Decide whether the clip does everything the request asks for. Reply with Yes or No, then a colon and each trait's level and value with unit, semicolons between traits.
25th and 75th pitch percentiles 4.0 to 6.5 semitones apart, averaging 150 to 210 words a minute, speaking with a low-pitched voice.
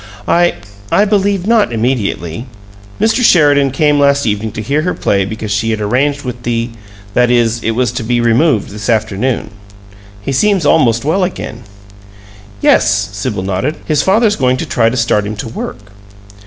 Yes: average, 5.2 semitones; average, 170 wpm; low, 120 Hz